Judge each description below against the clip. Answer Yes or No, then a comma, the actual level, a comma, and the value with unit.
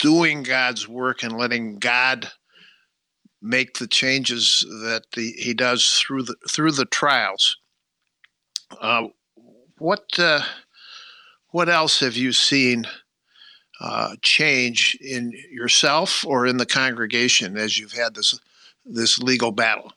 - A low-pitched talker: Yes, low, 125 Hz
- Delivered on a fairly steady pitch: Yes, narrow, 2.2 semitones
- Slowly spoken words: Yes, slow, 125 wpm